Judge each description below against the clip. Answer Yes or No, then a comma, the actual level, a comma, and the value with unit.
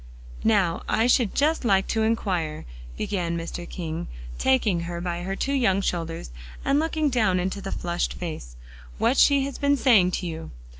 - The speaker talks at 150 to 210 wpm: Yes, average, 170 wpm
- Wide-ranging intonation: Yes, wide, 6.4 semitones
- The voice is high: Yes, high, 195 Hz